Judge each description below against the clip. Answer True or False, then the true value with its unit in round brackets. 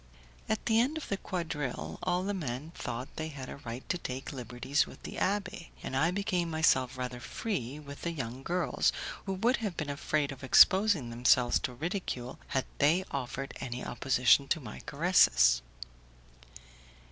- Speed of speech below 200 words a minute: True (170 wpm)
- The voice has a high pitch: False (145 Hz)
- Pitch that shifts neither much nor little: False (6.1 semitones)